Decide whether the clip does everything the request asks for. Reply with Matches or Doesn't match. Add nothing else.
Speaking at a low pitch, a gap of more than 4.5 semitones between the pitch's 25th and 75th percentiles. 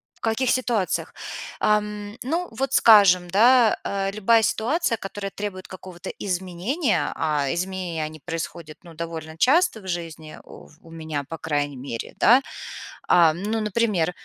Doesn't match